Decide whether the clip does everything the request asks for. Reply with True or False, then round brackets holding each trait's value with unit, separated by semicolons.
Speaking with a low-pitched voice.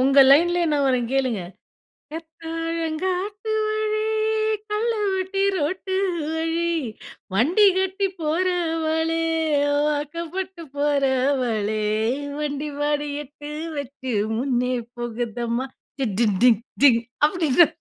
False (315 Hz)